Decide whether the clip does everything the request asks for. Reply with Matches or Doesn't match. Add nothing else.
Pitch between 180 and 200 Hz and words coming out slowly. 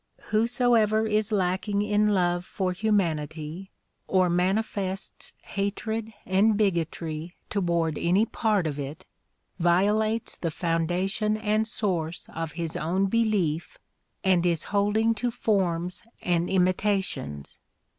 Matches